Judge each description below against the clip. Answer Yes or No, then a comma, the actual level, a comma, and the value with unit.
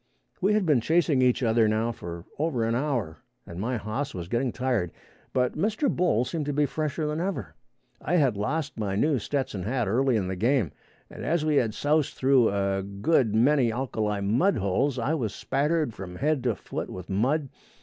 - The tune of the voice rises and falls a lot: Yes, wide, 5.9 semitones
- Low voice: Yes, low, 125 Hz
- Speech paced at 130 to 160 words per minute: No, average, 195 wpm